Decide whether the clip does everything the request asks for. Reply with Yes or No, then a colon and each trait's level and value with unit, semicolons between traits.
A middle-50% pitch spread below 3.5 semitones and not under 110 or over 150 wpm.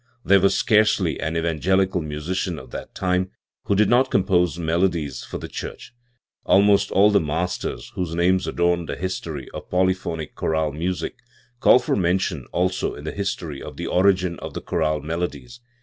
No: average, 2.8 semitones; average, 165 wpm